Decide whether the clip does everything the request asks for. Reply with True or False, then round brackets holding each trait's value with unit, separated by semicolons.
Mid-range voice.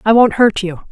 False (215 Hz)